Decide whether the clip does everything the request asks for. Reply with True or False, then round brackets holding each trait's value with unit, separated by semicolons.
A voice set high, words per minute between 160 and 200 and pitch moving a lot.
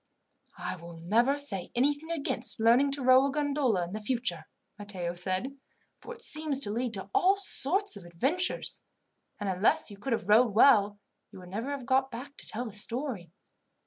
True (240 Hz; 180 wpm; 5.9 semitones)